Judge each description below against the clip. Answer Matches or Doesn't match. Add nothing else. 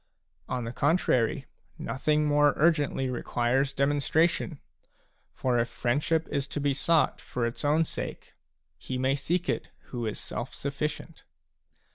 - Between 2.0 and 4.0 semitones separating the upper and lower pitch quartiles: Matches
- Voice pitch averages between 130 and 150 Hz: Matches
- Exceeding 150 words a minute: Doesn't match